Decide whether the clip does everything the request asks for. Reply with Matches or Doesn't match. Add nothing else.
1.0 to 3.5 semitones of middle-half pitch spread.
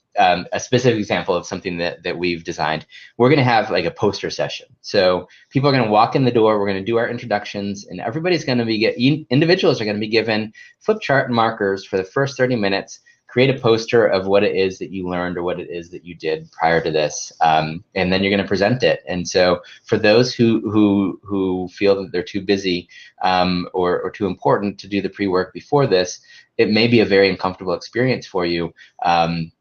Doesn't match